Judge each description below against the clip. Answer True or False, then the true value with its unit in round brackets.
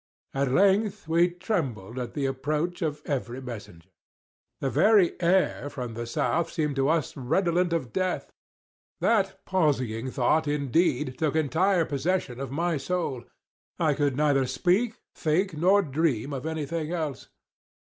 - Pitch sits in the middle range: True (150 Hz)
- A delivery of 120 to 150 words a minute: True (145 wpm)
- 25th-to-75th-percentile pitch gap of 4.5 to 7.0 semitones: True (4.9 semitones)